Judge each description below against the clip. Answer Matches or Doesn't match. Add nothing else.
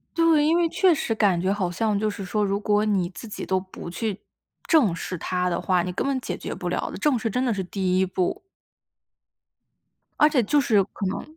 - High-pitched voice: Matches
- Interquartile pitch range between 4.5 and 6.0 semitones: Matches